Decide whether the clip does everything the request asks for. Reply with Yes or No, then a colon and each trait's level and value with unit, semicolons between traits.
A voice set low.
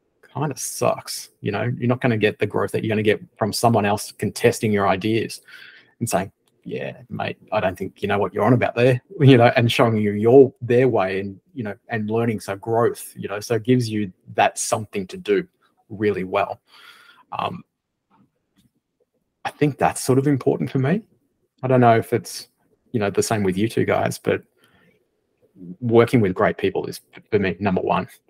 Yes: low, 115 Hz